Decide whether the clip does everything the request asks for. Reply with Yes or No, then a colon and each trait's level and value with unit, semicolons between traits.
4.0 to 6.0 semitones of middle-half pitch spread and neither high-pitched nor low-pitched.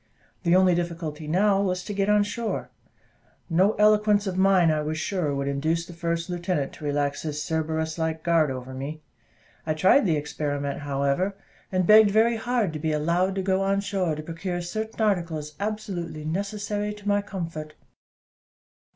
Yes: average, 4.4 semitones; medium, 175 Hz